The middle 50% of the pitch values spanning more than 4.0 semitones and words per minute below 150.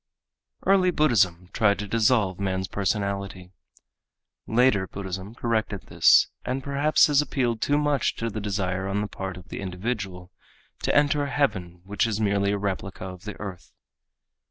No: average, 4.5 semitones; average, 155 wpm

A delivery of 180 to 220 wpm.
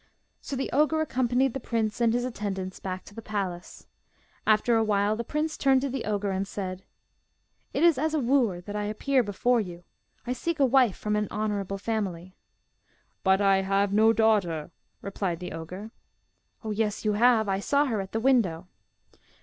Yes: average, 185 wpm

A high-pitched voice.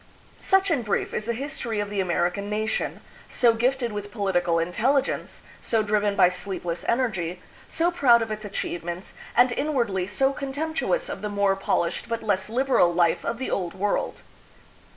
Yes: high, 210 Hz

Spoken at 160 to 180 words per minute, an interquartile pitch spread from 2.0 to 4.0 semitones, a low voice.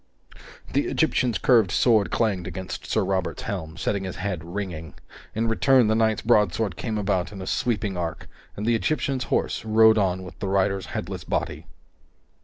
Yes: average, 170 wpm; average, 3.1 semitones; low, 100 Hz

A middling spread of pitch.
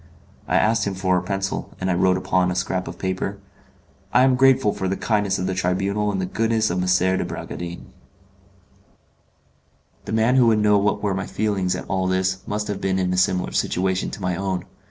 No: narrow, 2.0 semitones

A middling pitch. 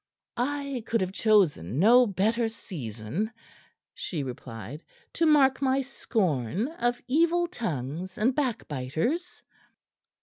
No: high, 220 Hz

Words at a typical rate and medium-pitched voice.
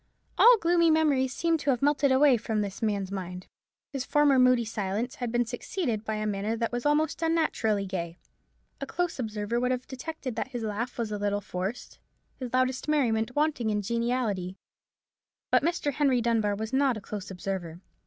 No: average, 180 wpm; high, 240 Hz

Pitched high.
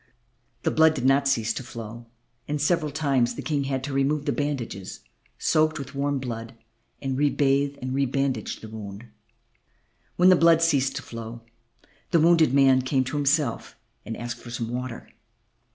No: low, 135 Hz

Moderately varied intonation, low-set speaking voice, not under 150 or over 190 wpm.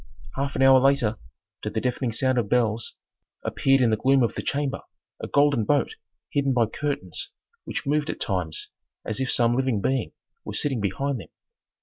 Yes: average, 3.5 semitones; low, 130 Hz; average, 185 wpm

